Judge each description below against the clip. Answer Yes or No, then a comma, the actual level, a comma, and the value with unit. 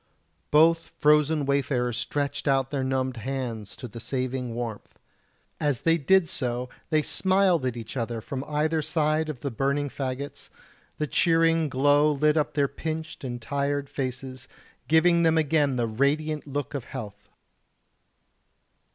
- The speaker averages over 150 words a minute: No, average, 145 wpm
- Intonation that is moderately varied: Yes, average, 3.0 semitones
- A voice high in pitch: No, medium, 140 Hz